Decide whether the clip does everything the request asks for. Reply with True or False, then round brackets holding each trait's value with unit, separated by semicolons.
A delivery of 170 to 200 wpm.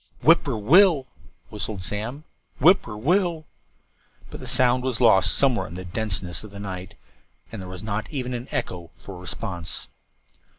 True (185 wpm)